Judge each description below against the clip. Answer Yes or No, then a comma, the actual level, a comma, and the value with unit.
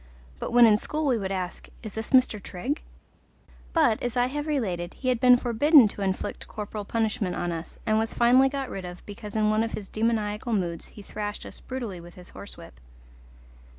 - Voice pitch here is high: Yes, high, 220 Hz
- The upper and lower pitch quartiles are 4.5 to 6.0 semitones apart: No, average, 4.0 semitones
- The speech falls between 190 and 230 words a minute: Yes, average, 200 wpm